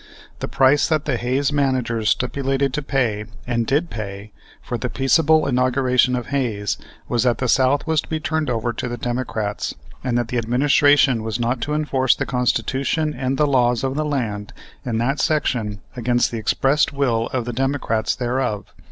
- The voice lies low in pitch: Yes, low, 125 Hz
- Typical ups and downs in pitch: Yes, average, 3.0 semitones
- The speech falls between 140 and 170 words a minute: No, average, 180 wpm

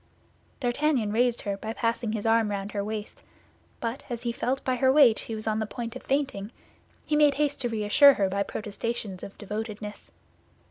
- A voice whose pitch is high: Yes, high, 230 Hz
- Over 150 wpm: Yes, average, 190 wpm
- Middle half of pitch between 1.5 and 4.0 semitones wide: Yes, average, 3.6 semitones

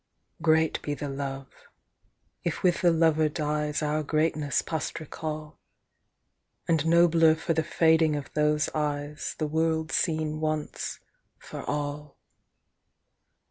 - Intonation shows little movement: Yes, narrow, 1.4 semitones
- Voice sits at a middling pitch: Yes, medium, 155 Hz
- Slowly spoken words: Yes, slow, 120 wpm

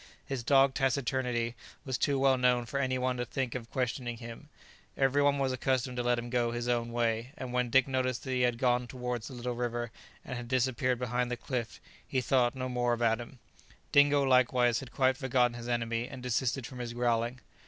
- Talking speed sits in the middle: No, fast, 210 wpm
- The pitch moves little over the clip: Yes, narrow, 1.6 semitones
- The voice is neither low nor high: No, low, 125 Hz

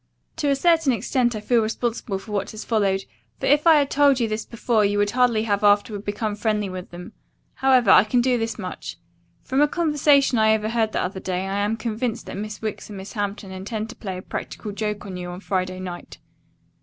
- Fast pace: Yes, fast, 220 wpm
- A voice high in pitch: Yes, high, 215 Hz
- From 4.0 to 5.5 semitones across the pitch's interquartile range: No, average, 3.4 semitones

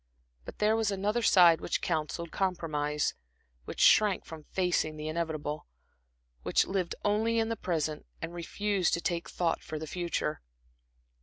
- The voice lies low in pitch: No, medium, 170 Hz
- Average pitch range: Yes, average, 4.2 semitones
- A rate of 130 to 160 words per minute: Yes, average, 150 wpm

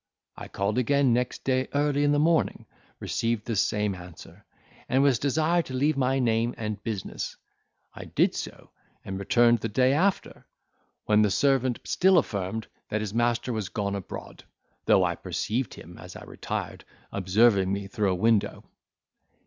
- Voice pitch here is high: No, low, 115 Hz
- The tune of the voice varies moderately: Yes, average, 4.6 semitones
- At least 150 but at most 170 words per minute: Yes, average, 165 wpm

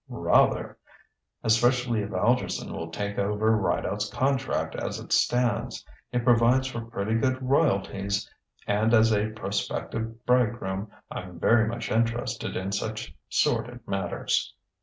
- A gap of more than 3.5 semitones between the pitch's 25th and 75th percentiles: No, average, 2.9 semitones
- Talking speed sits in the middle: No, slow, 125 wpm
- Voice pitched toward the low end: Yes, low, 110 Hz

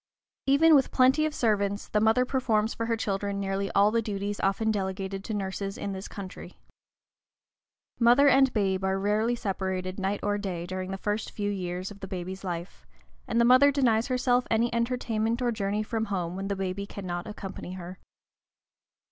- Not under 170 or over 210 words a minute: Yes, average, 180 wpm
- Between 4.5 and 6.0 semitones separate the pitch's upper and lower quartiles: No, average, 3.3 semitones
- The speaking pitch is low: No, high, 205 Hz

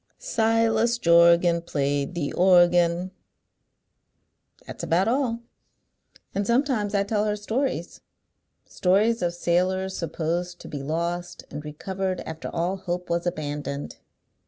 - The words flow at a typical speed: No, slow, 115 wpm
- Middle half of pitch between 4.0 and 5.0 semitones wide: No, average, 3.5 semitones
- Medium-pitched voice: Yes, medium, 180 Hz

